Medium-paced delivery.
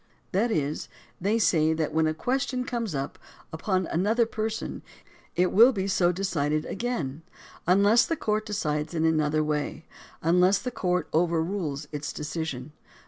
Yes: average, 145 wpm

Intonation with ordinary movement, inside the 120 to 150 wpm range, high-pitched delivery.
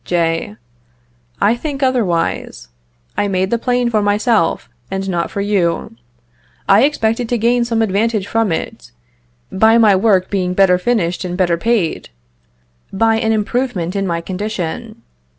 Yes: average, 4.0 semitones; average, 145 wpm; high, 205 Hz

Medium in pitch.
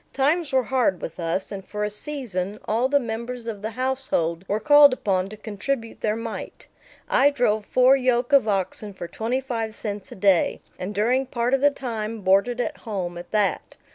No: high, 225 Hz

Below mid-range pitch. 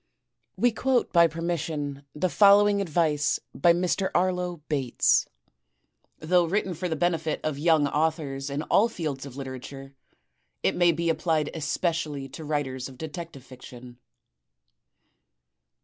No: medium, 160 Hz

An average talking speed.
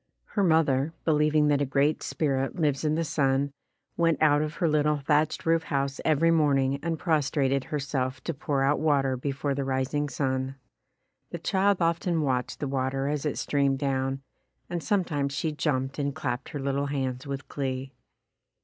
Yes: average, 170 wpm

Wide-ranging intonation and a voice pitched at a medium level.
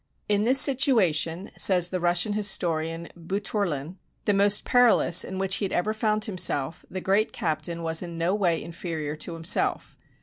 No: average, 3.8 semitones; medium, 180 Hz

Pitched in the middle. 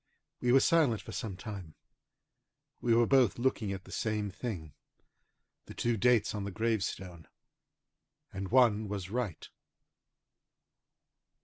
No: low, 110 Hz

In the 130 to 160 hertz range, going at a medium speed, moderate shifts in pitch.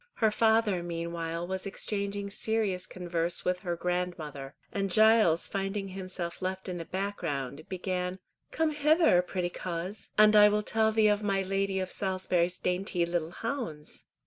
No: medium, 185 Hz; average, 150 wpm; average, 3.0 semitones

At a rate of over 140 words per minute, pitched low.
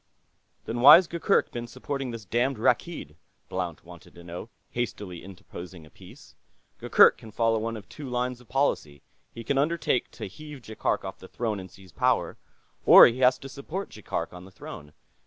Yes: average, 180 wpm; low, 115 Hz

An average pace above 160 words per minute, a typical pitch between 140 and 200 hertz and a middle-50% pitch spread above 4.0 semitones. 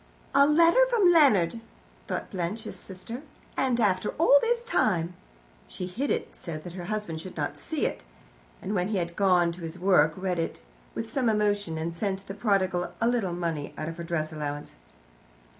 Yes: average, 185 wpm; high, 190 Hz; average, 5.1 semitones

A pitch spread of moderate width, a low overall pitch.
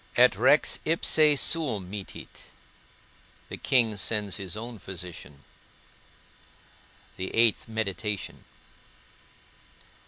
Yes: average, 3.9 semitones; low, 105 Hz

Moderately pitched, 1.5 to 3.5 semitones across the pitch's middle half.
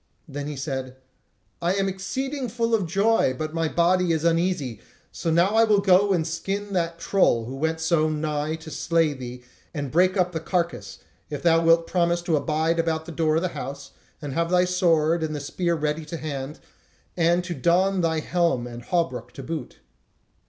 Yes: medium, 165 Hz; average, 3.0 semitones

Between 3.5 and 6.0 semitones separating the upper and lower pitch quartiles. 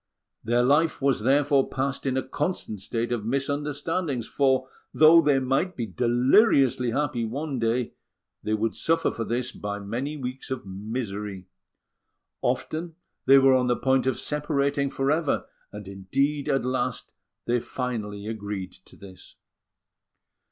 Yes: average, 3.9 semitones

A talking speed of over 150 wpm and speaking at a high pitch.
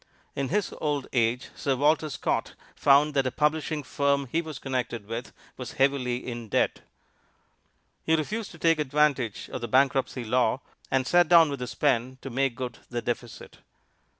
No: average, 170 wpm; low, 135 Hz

